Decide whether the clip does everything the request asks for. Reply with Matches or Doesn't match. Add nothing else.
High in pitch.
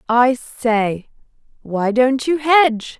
Matches